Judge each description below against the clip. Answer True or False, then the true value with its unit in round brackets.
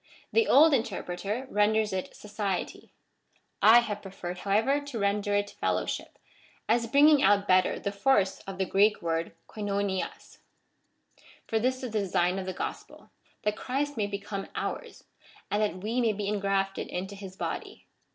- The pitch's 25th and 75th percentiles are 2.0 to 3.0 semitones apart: True (2.5 semitones)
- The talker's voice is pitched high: True (205 Hz)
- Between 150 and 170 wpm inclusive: True (160 wpm)